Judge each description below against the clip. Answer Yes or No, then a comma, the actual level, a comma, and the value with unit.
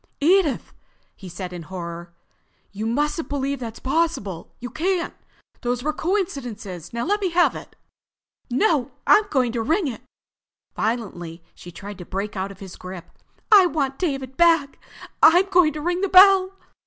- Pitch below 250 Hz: No, very high, 265 Hz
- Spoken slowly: No, average, 160 wpm